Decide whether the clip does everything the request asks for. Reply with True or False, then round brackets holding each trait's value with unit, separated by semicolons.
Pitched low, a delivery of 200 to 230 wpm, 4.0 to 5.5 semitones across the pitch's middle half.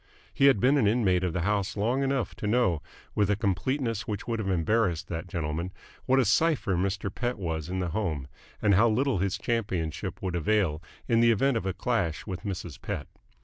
True (100 Hz; 205 wpm; 4.5 semitones)